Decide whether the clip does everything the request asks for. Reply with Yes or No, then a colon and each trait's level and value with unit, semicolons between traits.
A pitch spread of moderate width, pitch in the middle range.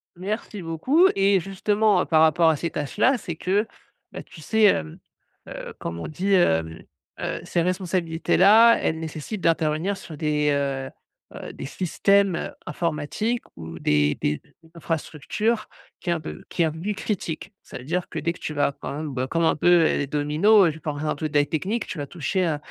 Yes: average, 4.7 semitones; medium, 165 Hz